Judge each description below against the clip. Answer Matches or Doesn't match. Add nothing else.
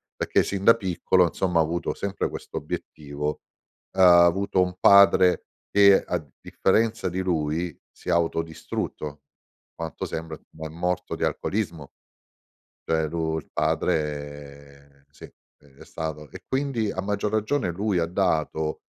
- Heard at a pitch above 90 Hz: Doesn't match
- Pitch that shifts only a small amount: Doesn't match